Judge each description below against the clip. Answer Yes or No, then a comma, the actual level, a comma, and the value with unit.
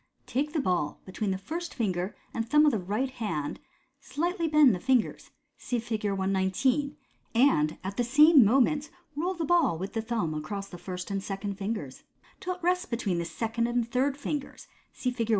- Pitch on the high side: Yes, high, 230 Hz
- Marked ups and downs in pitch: Yes, wide, 6.8 semitones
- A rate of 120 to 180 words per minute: No, average, 195 wpm